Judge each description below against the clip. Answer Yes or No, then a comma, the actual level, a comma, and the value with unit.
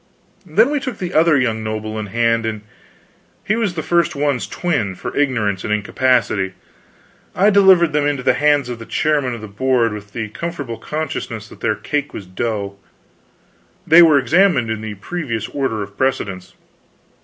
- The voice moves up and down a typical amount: No, wide, 6.3 semitones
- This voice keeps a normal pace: Yes, average, 175 wpm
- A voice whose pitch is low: Yes, low, 125 Hz